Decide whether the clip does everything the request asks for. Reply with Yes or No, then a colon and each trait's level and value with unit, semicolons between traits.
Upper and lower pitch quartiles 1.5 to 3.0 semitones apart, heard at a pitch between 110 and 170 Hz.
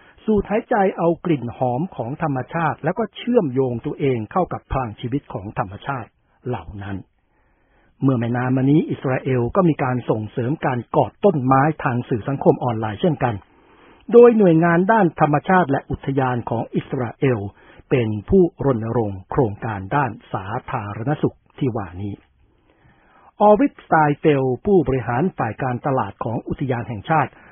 No: average, 5.2 semitones; low, 135 Hz